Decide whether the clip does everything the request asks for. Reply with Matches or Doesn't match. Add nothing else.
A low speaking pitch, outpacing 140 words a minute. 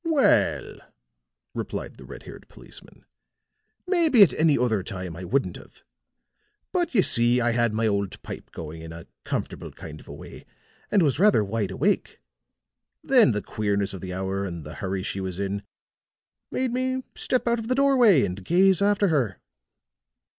Matches